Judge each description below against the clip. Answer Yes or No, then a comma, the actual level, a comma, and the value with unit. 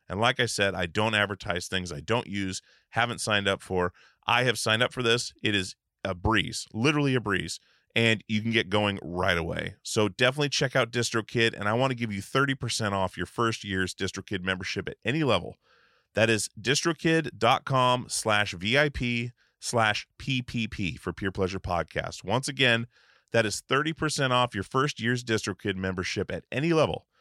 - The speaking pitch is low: Yes, low, 110 Hz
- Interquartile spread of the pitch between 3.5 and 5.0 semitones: Yes, average, 4.1 semitones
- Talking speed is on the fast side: No, average, 180 wpm